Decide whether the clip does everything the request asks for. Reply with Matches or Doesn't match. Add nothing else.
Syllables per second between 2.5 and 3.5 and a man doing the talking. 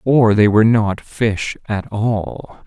Matches